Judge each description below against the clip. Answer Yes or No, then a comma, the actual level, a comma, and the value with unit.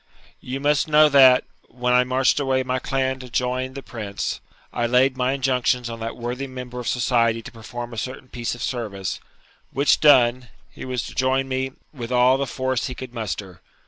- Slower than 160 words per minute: No, average, 195 wpm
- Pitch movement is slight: Yes, narrow, 1.7 semitones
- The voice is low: Yes, low, 125 Hz